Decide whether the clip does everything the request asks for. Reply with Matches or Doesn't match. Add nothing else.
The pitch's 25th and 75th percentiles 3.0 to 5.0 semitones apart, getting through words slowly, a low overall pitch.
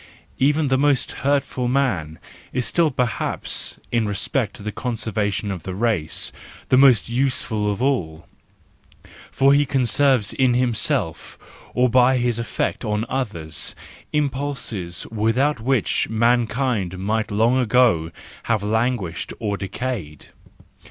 Matches